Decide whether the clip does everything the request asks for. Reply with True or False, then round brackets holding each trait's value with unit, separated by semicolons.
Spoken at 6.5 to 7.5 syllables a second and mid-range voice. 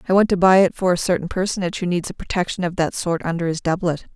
True (6.9 syllables/s; 180 Hz)